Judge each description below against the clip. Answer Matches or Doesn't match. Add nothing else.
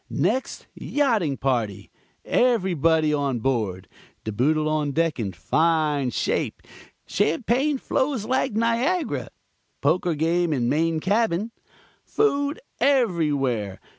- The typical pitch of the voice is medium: Matches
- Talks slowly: Matches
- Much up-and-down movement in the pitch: Matches